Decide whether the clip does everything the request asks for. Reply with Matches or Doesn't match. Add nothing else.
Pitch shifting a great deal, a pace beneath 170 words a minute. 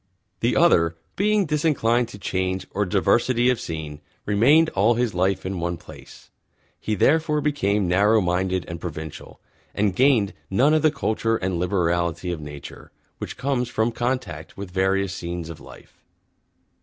Matches